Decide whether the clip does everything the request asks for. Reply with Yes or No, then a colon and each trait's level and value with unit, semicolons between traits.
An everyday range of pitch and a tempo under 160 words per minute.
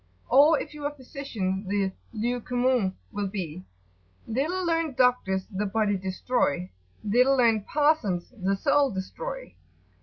No: wide, 6.3 semitones; average, 140 wpm